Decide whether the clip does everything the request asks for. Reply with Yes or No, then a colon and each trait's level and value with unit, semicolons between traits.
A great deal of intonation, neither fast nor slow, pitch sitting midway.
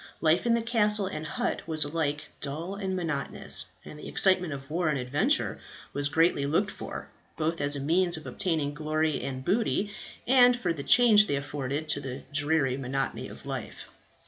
No: average, 4.7 semitones; average, 180 wpm; medium, 155 Hz